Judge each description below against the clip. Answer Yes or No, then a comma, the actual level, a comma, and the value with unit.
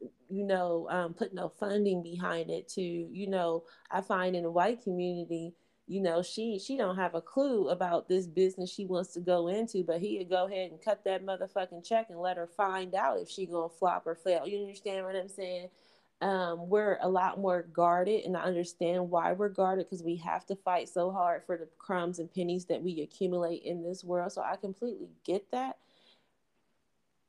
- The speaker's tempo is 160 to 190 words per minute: No, fast, 205 wpm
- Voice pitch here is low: No, medium, 180 Hz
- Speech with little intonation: Yes, narrow, 1.9 semitones